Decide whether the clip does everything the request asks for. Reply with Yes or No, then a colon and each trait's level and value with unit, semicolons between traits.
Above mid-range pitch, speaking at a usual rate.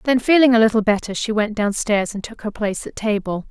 No: high, 215 Hz; fast, 240 wpm